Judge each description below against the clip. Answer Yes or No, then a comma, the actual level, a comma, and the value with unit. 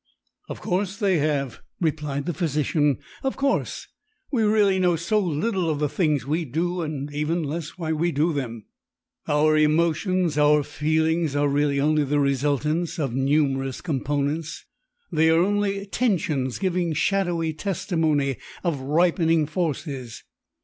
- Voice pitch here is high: No, medium, 155 Hz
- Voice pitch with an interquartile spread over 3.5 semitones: No, average, 3.2 semitones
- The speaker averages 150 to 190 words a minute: No, average, 140 wpm